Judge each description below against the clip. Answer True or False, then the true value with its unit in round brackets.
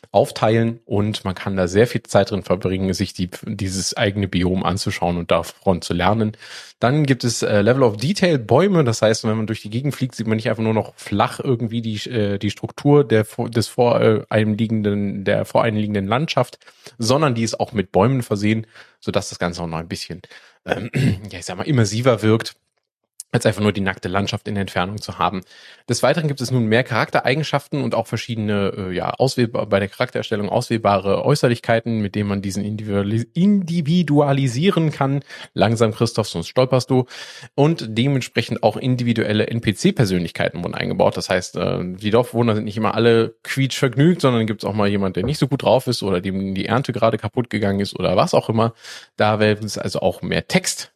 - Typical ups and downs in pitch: True (3.7 semitones)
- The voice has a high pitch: False (110 Hz)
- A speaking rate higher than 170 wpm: True (185 wpm)